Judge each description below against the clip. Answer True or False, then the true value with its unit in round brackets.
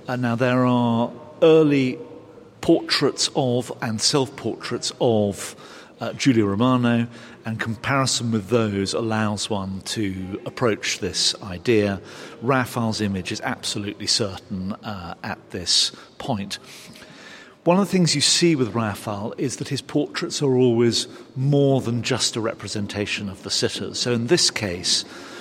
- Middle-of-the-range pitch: False (115 Hz)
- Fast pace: False (140 wpm)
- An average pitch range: True (3.7 semitones)